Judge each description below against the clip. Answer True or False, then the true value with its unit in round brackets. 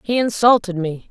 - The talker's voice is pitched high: True (205 Hz)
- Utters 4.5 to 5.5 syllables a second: True (5.0 syllables/s)